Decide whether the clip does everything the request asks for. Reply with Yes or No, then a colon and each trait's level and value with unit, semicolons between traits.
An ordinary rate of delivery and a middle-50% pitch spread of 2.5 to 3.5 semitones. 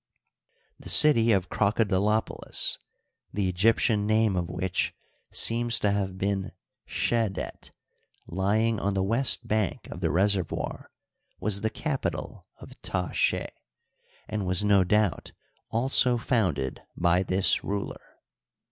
No: slow, 120 wpm; average, 3.0 semitones